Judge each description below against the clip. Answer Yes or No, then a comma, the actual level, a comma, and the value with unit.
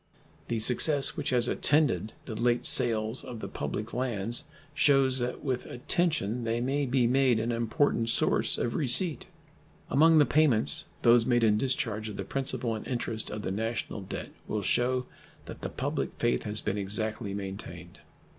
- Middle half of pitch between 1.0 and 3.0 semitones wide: No, average, 3.4 semitones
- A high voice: No, low, 120 Hz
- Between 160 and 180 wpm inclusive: Yes, average, 165 wpm